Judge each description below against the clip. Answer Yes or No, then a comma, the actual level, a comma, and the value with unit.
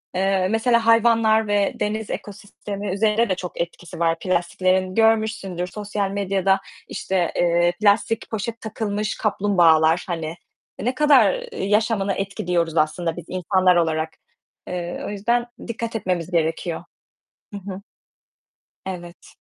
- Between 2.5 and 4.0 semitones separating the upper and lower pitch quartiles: Yes, average, 3.7 semitones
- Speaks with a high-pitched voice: Yes, high, 195 Hz